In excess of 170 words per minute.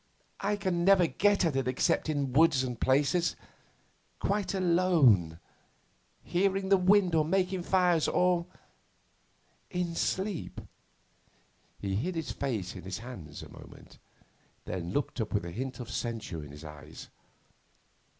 No: average, 140 wpm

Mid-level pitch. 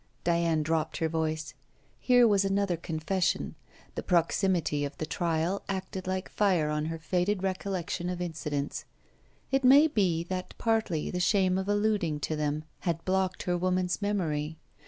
Yes: medium, 180 Hz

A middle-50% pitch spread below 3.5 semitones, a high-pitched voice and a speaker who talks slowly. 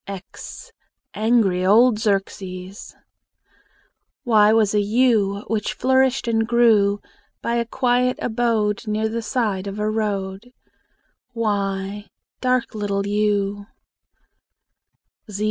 Yes: average, 2.7 semitones; high, 215 Hz; slow, 100 wpm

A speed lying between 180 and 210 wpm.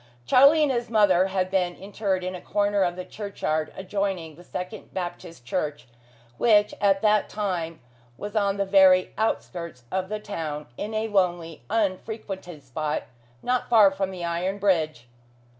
No: average, 160 wpm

